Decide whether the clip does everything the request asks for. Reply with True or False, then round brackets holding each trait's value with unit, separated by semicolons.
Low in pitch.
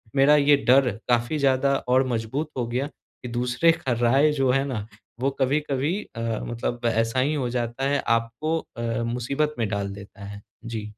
True (130 Hz)